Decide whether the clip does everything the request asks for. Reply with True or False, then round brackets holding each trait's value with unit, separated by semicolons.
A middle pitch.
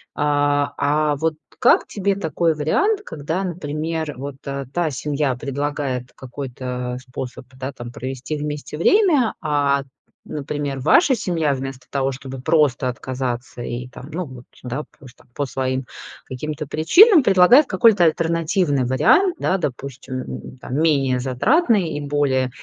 True (145 Hz)